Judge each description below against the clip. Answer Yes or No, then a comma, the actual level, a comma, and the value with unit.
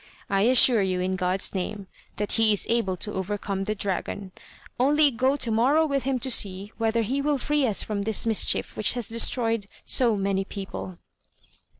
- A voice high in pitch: Yes, high, 215 Hz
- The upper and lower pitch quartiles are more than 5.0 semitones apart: No, average, 4.2 semitones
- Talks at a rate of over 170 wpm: Yes, average, 185 wpm